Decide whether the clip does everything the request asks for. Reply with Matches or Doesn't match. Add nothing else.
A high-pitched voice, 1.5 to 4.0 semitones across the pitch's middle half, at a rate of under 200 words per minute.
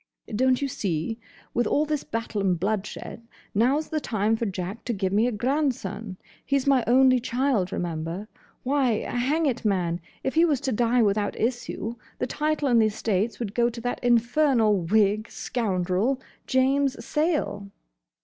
Doesn't match